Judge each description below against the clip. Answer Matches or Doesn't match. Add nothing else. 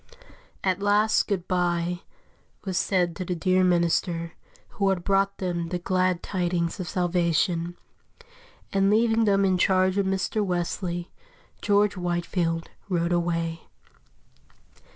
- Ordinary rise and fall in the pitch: Doesn't match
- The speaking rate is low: Matches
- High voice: Doesn't match